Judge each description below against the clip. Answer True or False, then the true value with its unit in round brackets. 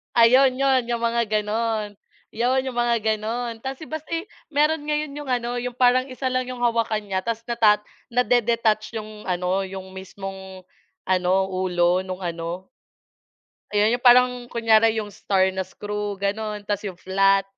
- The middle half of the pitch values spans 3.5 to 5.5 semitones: True (4.1 semitones)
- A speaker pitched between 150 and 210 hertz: False (220 Hz)